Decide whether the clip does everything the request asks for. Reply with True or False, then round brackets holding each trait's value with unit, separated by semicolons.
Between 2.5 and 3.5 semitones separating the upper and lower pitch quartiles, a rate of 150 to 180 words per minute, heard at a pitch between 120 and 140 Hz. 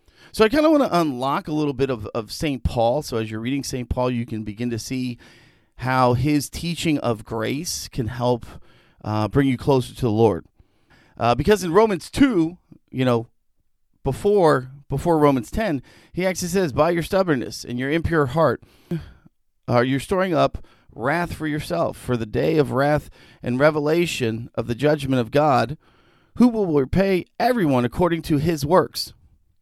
False (5.3 semitones; 175 wpm; 135 Hz)